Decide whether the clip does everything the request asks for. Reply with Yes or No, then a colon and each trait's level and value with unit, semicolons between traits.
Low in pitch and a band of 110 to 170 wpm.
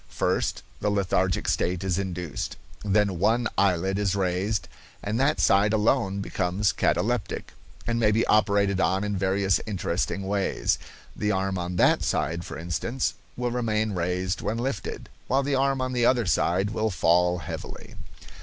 Yes: low, 100 Hz; average, 155 wpm